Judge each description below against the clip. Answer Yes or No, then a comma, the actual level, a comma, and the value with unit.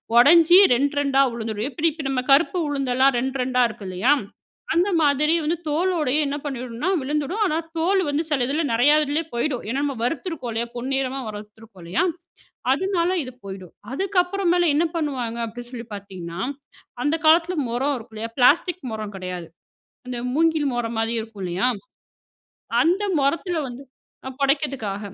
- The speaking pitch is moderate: No, very high, 270 Hz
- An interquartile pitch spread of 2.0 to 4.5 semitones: No, average, 5.3 semitones